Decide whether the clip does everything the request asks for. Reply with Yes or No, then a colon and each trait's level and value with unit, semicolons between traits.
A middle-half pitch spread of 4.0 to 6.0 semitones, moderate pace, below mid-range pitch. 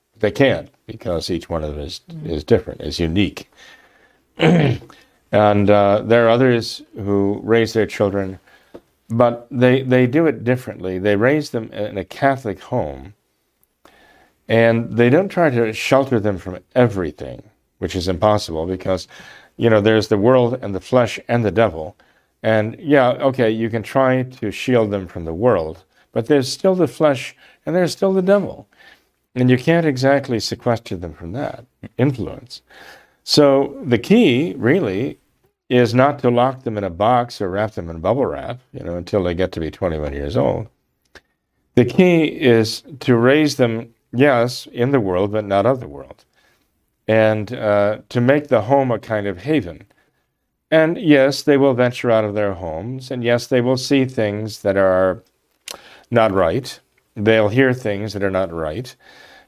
Yes: average, 4.4 semitones; average, 170 wpm; low, 115 Hz